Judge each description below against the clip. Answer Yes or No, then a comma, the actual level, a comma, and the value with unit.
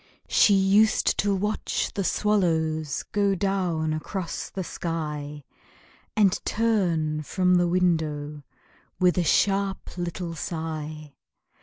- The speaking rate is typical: No, slow, 110 wpm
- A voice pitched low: No, medium, 175 Hz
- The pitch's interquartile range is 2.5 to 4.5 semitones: Yes, average, 3.8 semitones